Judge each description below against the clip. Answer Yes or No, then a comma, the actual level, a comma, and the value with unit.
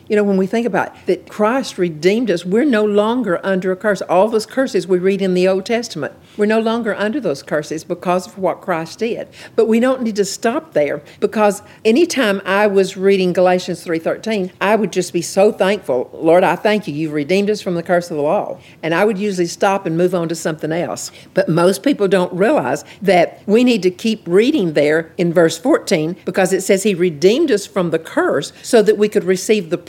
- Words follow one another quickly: Yes, fast, 225 wpm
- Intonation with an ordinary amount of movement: Yes, average, 3.2 semitones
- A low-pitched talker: No, high, 190 Hz